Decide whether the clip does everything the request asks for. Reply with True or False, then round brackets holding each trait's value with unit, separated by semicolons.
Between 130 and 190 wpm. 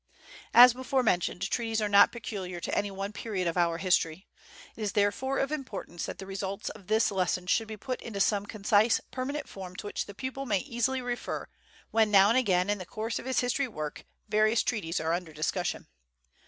False (205 wpm)